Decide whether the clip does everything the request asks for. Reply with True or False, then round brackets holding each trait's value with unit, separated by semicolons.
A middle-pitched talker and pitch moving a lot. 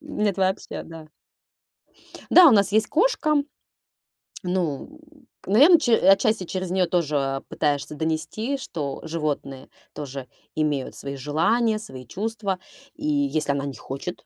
True (180 Hz; 7.2 semitones)